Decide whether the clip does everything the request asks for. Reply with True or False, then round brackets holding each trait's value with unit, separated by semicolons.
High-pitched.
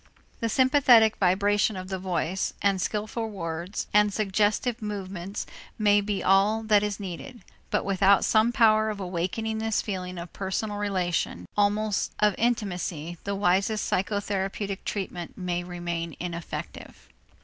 True (200 Hz)